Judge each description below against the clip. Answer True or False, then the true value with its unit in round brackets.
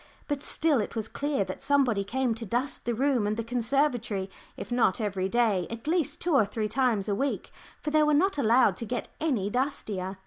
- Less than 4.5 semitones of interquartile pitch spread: False (5.1 semitones)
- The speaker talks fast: True (210 wpm)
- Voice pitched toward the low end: False (240 Hz)